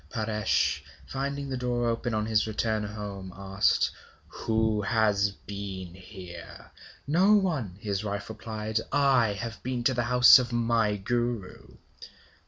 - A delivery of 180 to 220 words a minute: No, slow, 135 wpm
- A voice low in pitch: Yes, low, 110 Hz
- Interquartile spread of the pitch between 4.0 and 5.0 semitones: No, average, 3.1 semitones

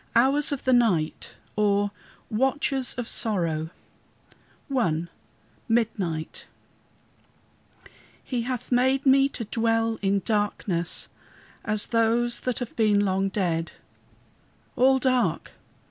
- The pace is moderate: No, slow, 100 wpm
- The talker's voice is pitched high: Yes, high, 225 Hz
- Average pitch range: Yes, average, 4.1 semitones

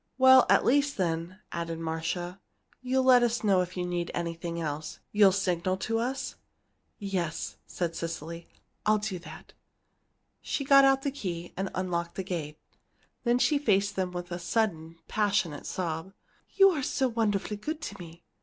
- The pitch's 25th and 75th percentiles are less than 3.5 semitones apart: No, average, 5.3 semitones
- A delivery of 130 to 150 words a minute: No, average, 160 wpm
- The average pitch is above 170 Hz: Yes, medium, 185 Hz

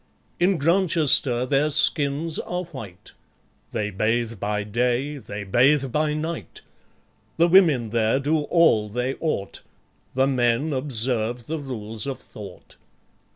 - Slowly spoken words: Yes, slow, 125 wpm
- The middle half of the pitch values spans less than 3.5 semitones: No, average, 5.3 semitones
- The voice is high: No, low, 130 Hz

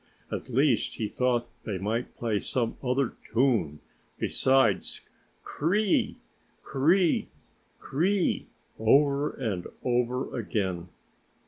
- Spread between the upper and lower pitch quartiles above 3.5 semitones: Yes, average, 3.9 semitones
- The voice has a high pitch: No, low, 125 Hz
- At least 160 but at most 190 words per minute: No, average, 140 wpm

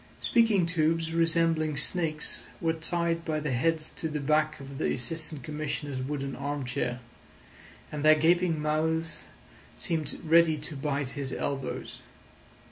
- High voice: No, medium, 155 Hz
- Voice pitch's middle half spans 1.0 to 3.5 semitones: Yes, narrow, 2.4 semitones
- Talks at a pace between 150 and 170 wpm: No, slow, 135 wpm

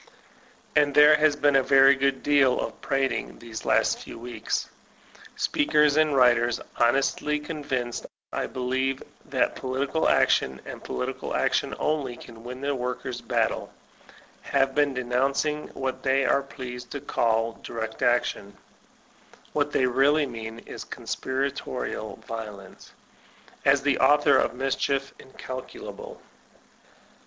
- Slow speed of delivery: Yes, slow, 130 wpm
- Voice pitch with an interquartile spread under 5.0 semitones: Yes, narrow, 2.6 semitones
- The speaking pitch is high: No, low, 135 Hz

